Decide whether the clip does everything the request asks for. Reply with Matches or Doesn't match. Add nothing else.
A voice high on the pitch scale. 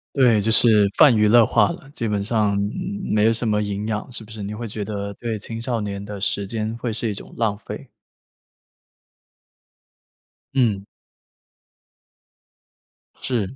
Doesn't match